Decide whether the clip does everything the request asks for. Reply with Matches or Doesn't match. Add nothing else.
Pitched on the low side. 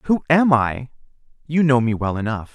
Matches